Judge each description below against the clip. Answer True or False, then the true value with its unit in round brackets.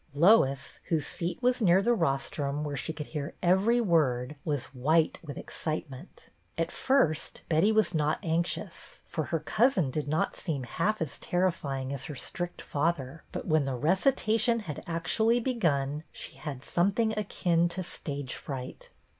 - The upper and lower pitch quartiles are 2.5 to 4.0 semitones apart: False (4.9 semitones)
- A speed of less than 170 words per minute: True (155 wpm)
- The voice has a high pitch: False (165 Hz)